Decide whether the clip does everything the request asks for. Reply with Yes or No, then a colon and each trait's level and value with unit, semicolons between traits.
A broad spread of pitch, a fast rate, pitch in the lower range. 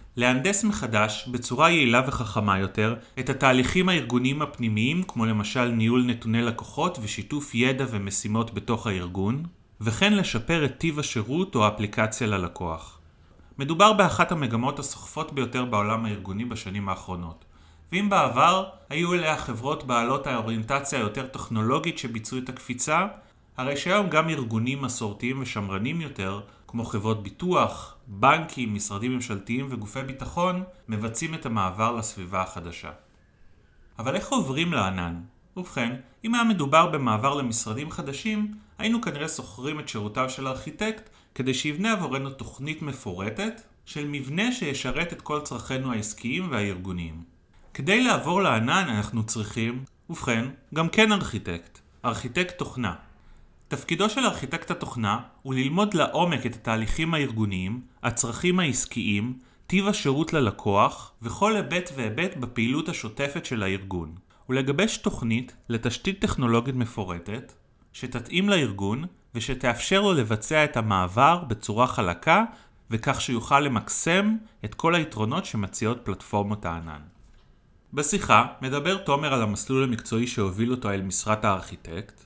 No: wide, 6.1 semitones; average, 120 wpm; low, 125 Hz